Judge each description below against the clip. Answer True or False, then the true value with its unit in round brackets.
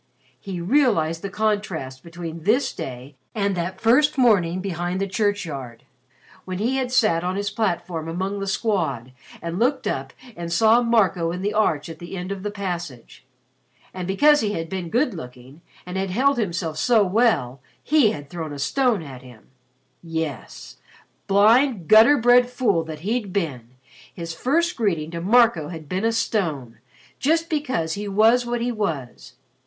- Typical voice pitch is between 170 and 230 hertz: True (190 Hz)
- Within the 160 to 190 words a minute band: True (170 wpm)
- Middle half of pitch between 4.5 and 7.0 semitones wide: True (5.6 semitones)